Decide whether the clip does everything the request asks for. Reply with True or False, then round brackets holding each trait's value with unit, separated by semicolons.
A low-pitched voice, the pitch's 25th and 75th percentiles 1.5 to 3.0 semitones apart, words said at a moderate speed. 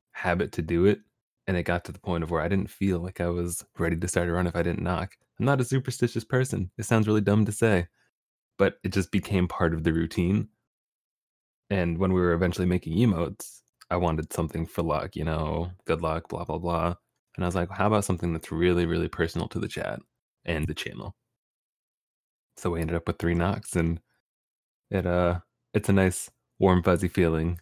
False (90 Hz; 2.6 semitones; 215 wpm)